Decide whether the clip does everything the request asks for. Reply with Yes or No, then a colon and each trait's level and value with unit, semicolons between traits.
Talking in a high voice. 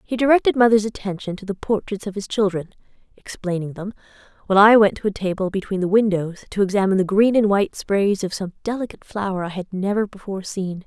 Yes: high, 200 Hz